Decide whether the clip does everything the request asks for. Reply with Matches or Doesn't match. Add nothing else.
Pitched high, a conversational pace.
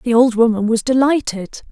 Matches